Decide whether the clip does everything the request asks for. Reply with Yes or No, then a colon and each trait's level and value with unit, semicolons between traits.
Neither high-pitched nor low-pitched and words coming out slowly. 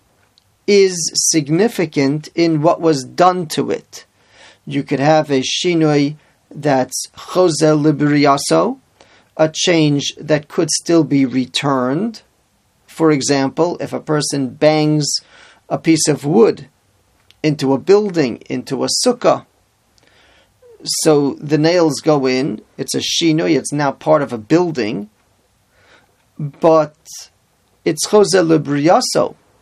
Yes: medium, 150 Hz; slow, 115 wpm